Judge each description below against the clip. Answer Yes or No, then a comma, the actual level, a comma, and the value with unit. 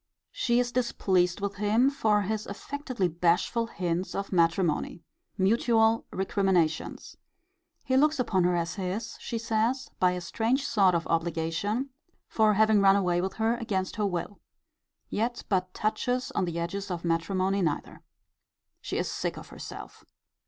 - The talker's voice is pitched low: No, high, 200 Hz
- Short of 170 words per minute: Yes, average, 150 wpm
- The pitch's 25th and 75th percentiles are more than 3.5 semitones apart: Yes, average, 4.3 semitones